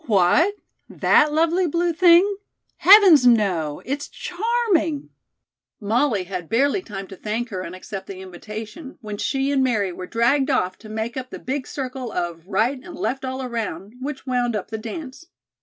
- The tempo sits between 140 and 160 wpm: No, average, 175 wpm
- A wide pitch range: Yes, wide, 6.2 semitones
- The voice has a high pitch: Yes, very high, 250 Hz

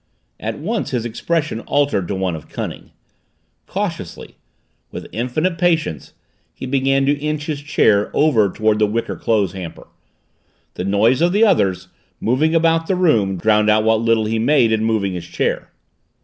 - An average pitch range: No, wide, 6.2 semitones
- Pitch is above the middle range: No, low, 115 Hz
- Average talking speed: Yes, average, 165 wpm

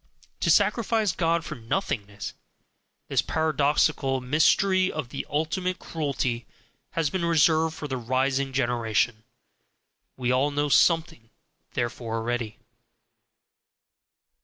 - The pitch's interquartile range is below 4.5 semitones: No, average, 5.0 semitones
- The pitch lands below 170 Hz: Yes, medium, 140 Hz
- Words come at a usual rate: No, slow, 105 wpm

